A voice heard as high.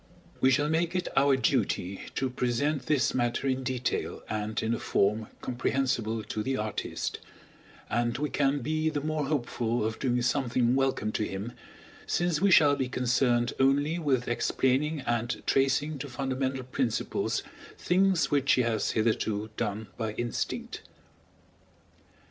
No: low, 130 Hz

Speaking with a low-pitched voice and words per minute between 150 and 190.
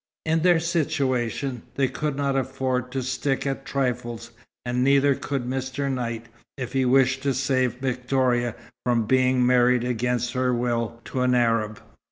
Yes: low, 130 Hz; average, 155 wpm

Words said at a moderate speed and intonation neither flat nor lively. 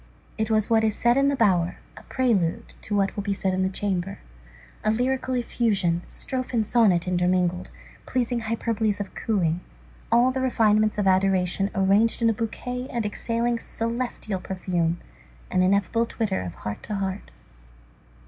Yes: average, 165 wpm; average, 3.7 semitones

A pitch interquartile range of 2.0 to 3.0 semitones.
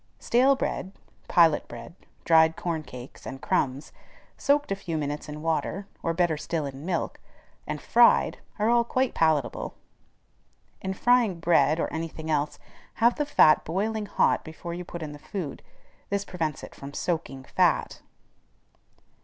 No: average, 4.6 semitones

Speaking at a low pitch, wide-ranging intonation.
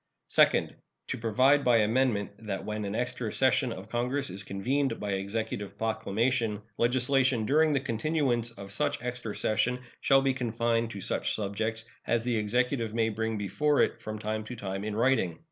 No: low, 115 Hz; average, 3.2 semitones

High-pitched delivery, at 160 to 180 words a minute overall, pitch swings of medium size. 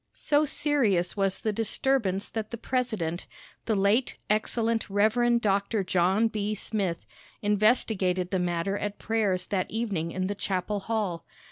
No: high, 205 Hz; average, 140 wpm; average, 3.2 semitones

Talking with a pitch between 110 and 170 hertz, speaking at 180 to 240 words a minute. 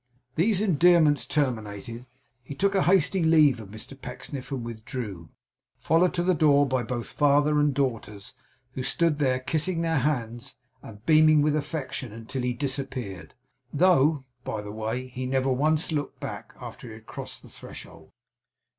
No: low, 135 Hz; average, 160 wpm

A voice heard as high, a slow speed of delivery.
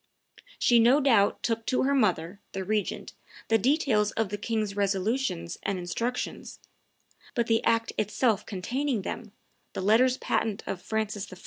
No: high, 220 Hz; average, 150 wpm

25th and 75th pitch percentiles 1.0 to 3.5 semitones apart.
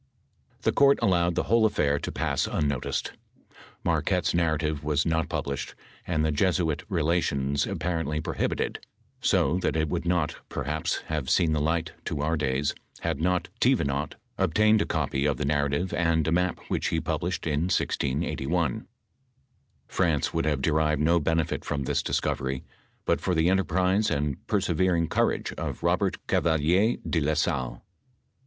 Yes: average, 3.2 semitones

